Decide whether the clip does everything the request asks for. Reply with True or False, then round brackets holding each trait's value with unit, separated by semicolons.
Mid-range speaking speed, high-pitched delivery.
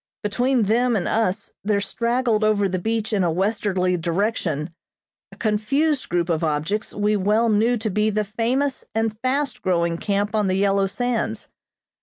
True (165 wpm; 210 Hz)